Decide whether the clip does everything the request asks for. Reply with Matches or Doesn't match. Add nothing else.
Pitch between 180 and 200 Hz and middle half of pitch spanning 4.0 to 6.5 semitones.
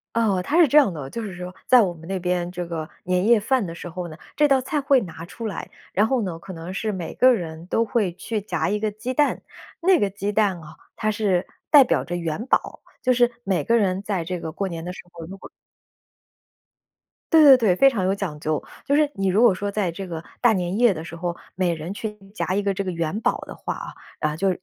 Matches